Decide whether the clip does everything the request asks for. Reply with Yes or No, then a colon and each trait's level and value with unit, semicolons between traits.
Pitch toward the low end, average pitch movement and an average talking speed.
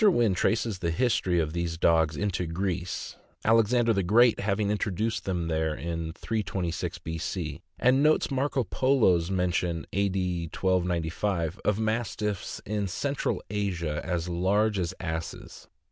Yes: very low, 95 Hz; average, 4.2 semitones; average, 145 wpm